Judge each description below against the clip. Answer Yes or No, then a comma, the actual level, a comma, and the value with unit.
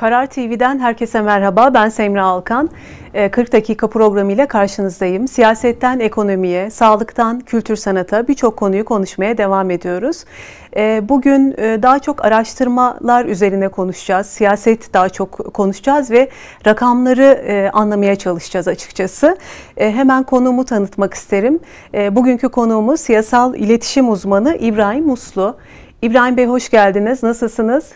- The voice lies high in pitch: Yes, high, 225 Hz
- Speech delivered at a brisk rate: No, average, 115 wpm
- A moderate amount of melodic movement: Yes, average, 3.7 semitones